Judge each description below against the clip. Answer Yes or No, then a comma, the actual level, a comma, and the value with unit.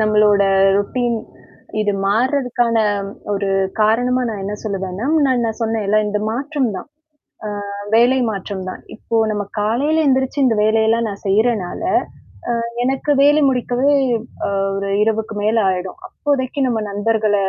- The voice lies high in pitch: Yes, high, 225 Hz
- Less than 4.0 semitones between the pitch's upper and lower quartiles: Yes, average, 3.6 semitones